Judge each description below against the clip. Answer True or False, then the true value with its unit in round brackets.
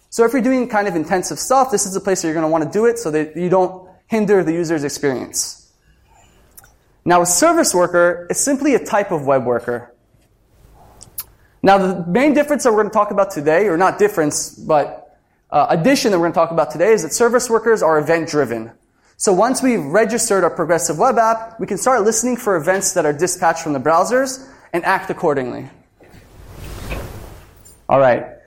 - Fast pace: True (200 wpm)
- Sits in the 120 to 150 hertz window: False (180 Hz)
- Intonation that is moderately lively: False (6.4 semitones)